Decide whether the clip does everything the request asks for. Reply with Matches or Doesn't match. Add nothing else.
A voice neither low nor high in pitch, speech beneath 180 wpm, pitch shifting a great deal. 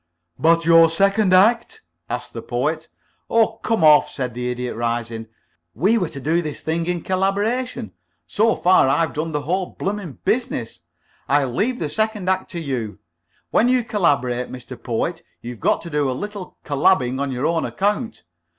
Matches